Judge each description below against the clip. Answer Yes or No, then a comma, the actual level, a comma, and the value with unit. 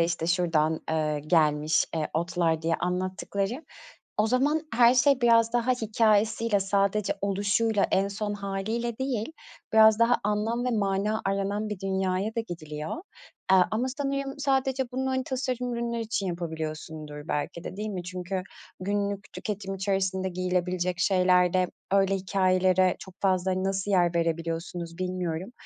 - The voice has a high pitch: Yes, high, 195 Hz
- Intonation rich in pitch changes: No, average, 3.8 semitones